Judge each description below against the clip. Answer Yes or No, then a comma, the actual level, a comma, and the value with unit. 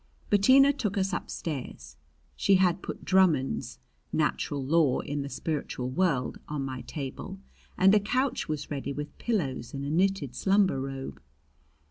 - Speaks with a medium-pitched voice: Yes, medium, 155 Hz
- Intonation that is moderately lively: No, wide, 6.1 semitones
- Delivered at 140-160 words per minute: Yes, average, 145 wpm